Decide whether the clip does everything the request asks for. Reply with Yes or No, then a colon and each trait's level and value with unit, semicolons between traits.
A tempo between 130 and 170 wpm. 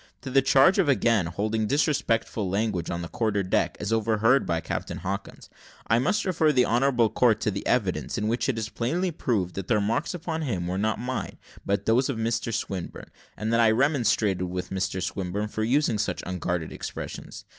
No: average, 195 wpm